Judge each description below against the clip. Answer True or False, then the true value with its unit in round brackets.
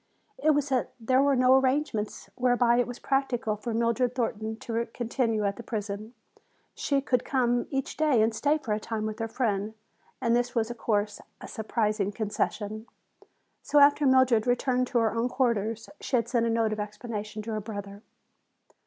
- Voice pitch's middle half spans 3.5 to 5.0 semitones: False (2.7 semitones)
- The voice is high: True (235 Hz)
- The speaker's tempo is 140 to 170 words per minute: False (185 wpm)